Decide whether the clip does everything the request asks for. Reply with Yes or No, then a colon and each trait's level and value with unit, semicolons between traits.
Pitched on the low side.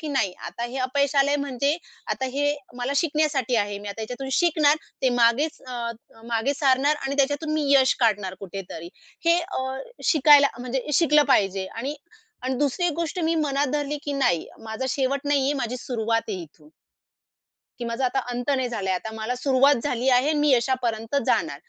No: very high, 260 Hz